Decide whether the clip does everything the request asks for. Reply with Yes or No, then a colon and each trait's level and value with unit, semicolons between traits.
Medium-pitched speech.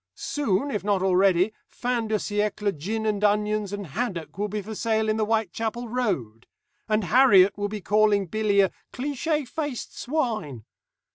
No: high, 210 Hz